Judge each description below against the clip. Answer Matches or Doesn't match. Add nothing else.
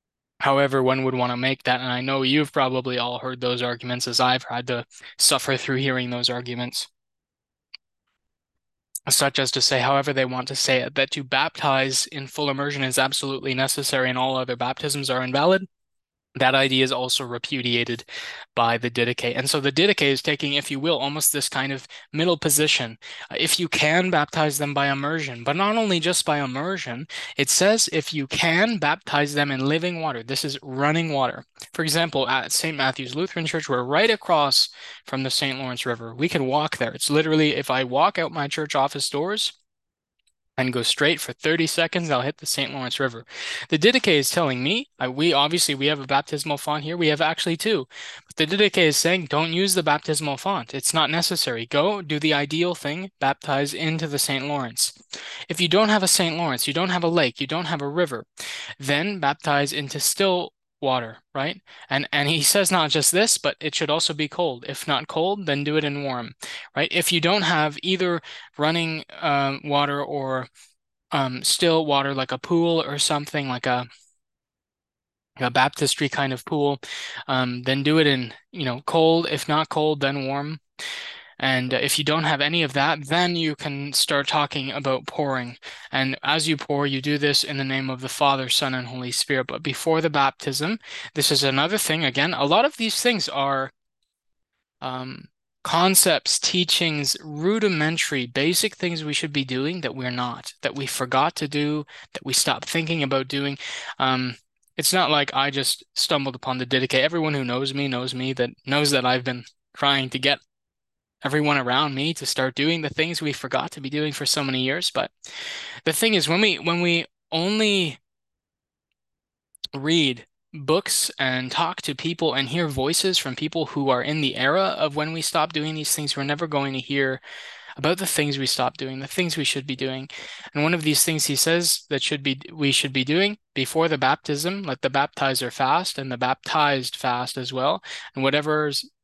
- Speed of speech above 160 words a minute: Matches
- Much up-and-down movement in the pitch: Doesn't match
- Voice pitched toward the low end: Doesn't match